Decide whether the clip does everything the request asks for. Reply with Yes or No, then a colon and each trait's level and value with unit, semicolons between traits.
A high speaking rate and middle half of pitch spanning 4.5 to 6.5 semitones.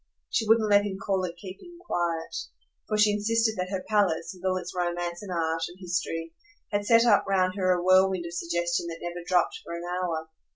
No: fast, 210 wpm; average, 2.9 semitones